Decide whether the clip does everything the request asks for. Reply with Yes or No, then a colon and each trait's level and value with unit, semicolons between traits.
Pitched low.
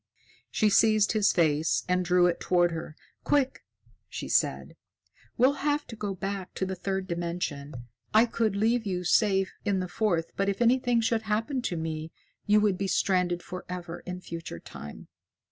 No: high, 190 Hz